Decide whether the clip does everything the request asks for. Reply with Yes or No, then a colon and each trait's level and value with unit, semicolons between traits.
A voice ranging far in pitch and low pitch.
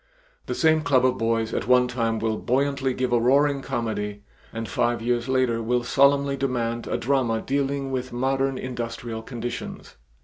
No: average, 2.7 semitones; low, 125 Hz